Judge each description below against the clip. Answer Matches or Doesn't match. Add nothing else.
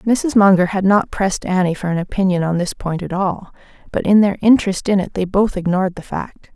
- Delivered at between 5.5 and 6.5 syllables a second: Matches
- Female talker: Matches